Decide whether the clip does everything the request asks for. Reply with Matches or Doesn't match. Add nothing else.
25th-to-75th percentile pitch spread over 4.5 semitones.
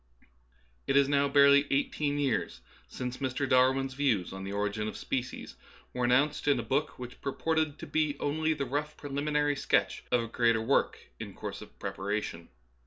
Doesn't match